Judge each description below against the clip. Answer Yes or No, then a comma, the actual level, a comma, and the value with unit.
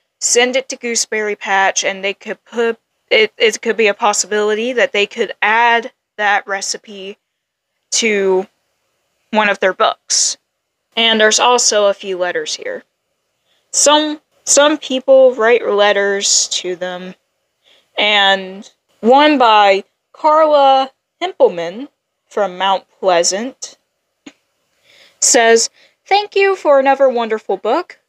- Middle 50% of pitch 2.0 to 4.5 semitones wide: No, wide, 5.4 semitones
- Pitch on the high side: Yes, high, 225 Hz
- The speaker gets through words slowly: Yes, slow, 120 wpm